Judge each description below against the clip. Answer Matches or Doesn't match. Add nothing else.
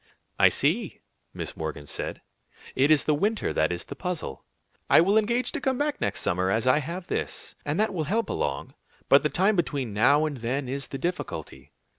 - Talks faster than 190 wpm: Matches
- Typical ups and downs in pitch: Doesn't match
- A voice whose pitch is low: Doesn't match